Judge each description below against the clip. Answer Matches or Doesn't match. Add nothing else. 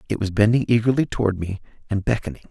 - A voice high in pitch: Doesn't match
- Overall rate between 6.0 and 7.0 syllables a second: Matches